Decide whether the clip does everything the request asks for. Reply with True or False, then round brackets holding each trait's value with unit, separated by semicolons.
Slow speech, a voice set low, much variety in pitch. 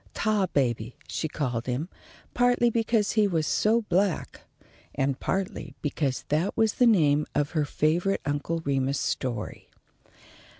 False (130 wpm; 155 Hz; 6.8 semitones)